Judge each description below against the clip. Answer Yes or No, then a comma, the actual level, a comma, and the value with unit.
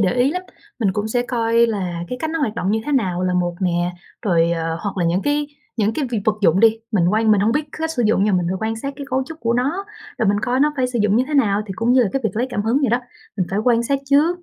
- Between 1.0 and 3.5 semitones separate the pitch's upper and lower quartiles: No, average, 5.2 semitones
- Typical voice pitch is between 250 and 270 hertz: No, high, 225 Hz